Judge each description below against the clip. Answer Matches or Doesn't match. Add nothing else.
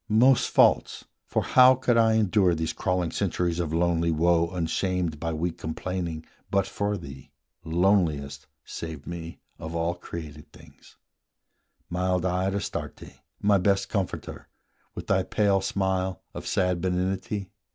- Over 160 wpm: Doesn't match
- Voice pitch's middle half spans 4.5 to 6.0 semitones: Doesn't match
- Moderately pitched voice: Doesn't match